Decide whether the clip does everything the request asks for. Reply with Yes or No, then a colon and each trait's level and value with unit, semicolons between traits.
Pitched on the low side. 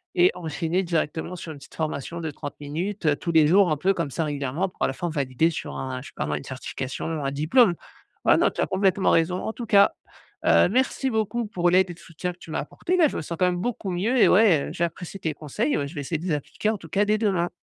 No: medium, 170 Hz